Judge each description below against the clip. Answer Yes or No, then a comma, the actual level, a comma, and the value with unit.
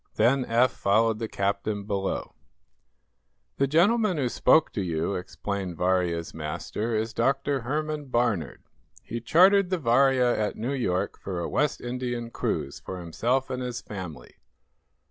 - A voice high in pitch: No, low, 115 Hz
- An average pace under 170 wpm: Yes, average, 145 wpm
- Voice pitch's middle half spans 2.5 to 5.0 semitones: No, wide, 5.4 semitones